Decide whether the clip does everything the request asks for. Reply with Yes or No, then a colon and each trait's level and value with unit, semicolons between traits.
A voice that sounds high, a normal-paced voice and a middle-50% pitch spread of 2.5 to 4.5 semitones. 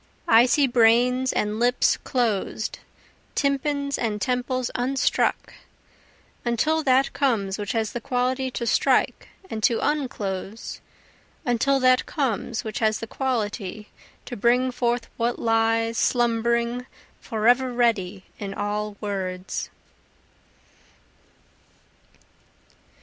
No: high, 235 Hz; slow, 105 wpm; average, 2.8 semitones